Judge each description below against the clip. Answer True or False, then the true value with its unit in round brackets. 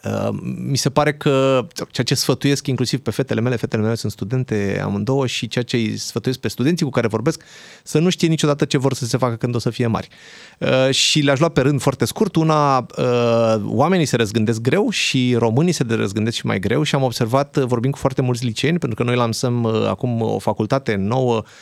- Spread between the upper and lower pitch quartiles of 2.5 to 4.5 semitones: True (3.7 semitones)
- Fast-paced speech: True (210 wpm)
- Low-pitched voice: True (130 Hz)